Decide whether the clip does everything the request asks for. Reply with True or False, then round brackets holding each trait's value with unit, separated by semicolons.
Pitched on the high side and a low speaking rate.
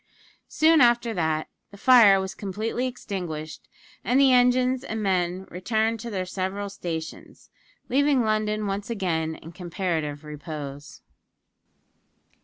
True (200 Hz; 120 wpm)